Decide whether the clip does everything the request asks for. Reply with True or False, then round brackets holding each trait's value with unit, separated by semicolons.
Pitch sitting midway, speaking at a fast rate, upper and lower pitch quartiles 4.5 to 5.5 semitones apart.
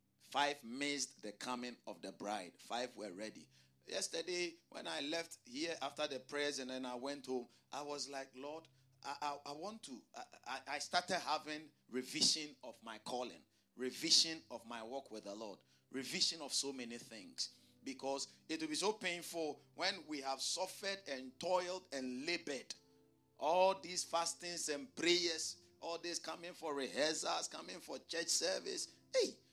False (145 Hz; 165 wpm; 4.8 semitones)